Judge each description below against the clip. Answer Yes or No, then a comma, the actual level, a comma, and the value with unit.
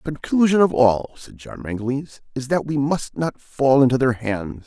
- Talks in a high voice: No, low, 135 Hz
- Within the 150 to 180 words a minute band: No, fast, 205 wpm